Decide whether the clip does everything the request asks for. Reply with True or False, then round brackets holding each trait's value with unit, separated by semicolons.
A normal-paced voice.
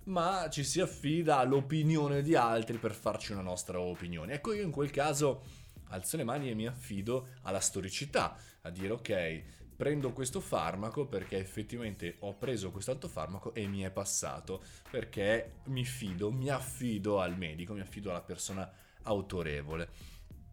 True (155 wpm)